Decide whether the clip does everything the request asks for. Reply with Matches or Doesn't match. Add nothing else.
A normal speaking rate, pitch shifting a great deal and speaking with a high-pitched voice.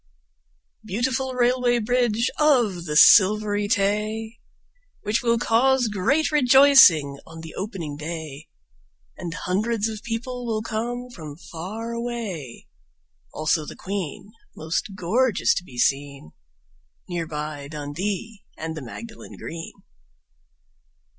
Doesn't match